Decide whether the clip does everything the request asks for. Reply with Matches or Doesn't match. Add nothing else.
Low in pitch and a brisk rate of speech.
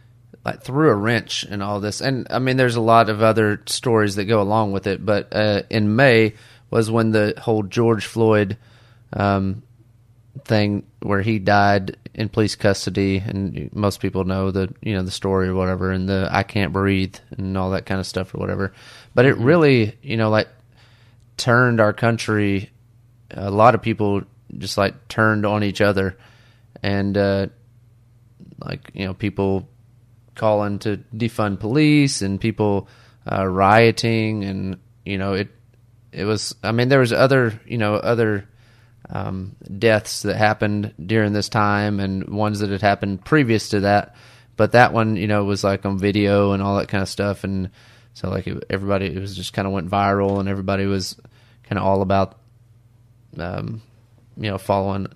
Doesn't match